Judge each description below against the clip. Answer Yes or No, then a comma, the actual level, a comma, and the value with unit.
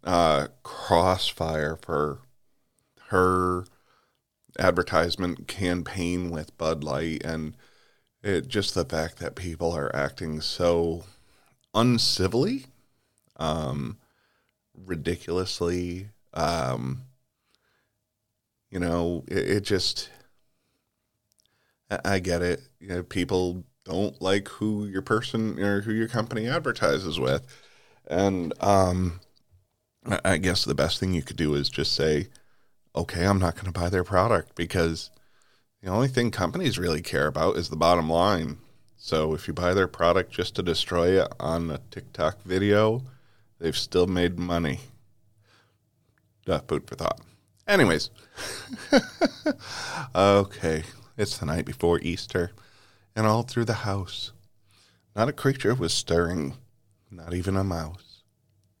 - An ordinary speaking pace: No, slow, 125 wpm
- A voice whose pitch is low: Yes, very low, 95 Hz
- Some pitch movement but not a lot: Yes, average, 3.6 semitones